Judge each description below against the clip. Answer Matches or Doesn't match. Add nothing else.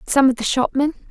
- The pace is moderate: Doesn't match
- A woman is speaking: Matches